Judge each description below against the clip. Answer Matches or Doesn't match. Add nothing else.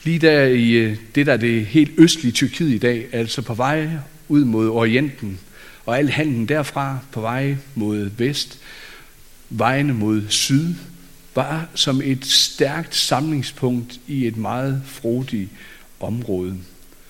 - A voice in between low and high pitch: Doesn't match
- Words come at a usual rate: Doesn't match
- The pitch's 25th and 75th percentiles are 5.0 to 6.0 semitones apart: Doesn't match